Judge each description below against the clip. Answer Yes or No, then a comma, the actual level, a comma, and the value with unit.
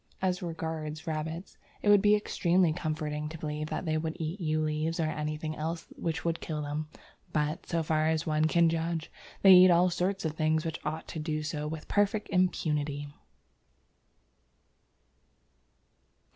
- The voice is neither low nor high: Yes, medium, 160 Hz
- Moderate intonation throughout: No, narrow, 1.8 semitones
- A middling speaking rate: Yes, average, 165 wpm